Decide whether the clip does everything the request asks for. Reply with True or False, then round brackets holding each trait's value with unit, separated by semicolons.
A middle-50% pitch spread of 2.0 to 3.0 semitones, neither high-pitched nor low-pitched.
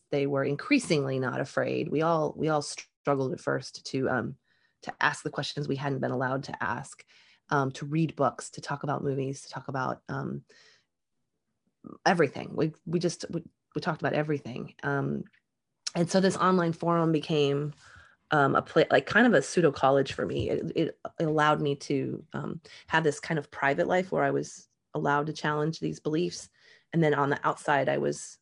True (2.4 semitones; 150 Hz)